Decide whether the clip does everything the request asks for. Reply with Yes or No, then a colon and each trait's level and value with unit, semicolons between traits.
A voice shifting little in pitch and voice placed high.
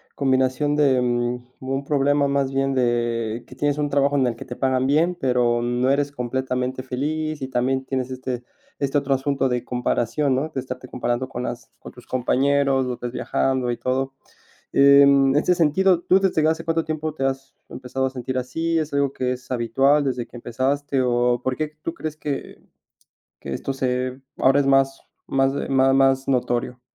No: narrow, 2.1 semitones; low, 135 Hz